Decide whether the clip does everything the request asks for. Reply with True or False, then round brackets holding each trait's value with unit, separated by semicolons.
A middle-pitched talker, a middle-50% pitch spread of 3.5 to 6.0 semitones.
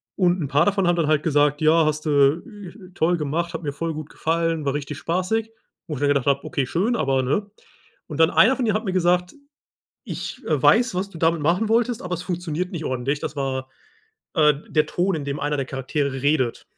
True (160 Hz; 3.9 semitones)